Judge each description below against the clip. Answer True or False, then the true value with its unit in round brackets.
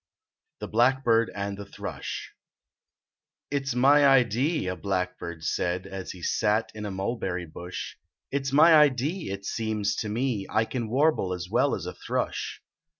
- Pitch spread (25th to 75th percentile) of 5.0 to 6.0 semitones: True (5.6 semitones)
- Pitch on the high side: False (110 Hz)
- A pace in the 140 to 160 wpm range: False (170 wpm)